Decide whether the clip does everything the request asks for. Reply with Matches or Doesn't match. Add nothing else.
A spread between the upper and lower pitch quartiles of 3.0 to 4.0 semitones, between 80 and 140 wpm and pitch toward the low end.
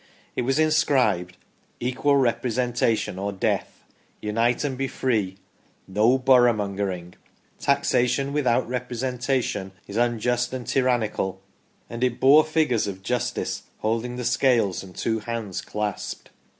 Matches